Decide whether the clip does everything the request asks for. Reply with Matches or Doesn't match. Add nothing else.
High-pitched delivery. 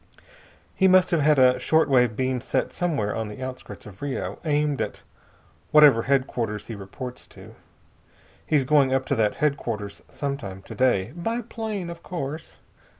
Doesn't match